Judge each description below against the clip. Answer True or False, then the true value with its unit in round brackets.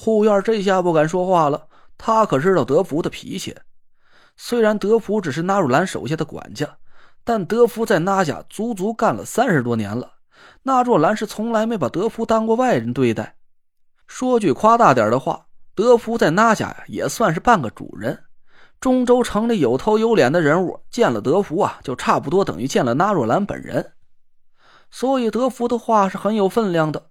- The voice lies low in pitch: False (220 Hz)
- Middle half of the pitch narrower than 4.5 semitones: True (3.4 semitones)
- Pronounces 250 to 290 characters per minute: True (275 characters per minute)